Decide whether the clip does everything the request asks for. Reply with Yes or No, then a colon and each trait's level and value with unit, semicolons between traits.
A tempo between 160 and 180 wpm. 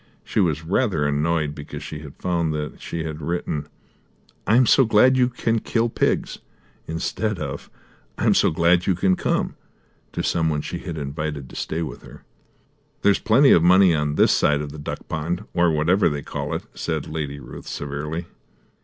No: average, 190 wpm